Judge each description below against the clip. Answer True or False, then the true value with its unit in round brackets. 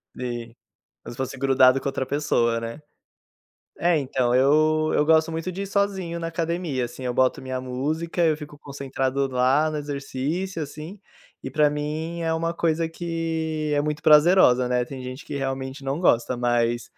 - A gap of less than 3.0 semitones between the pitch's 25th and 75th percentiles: False (3.8 semitones)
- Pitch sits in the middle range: True (145 Hz)